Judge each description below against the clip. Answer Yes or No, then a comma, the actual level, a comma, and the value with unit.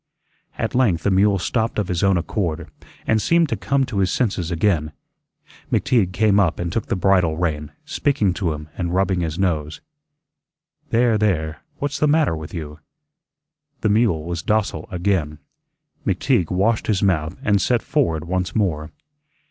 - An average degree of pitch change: Yes, average, 4.6 semitones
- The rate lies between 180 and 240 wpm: No, average, 165 wpm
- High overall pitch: No, very low, 95 Hz